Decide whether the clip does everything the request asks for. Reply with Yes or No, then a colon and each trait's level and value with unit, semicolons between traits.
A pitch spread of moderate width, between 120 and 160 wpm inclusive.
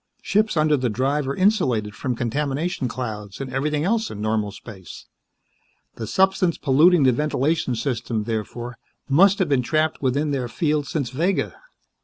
Yes: average, 4.8 semitones; average, 155 wpm